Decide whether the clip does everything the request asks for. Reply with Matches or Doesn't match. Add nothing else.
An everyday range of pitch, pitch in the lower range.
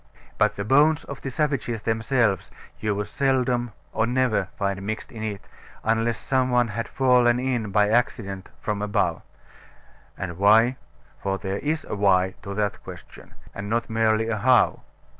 Matches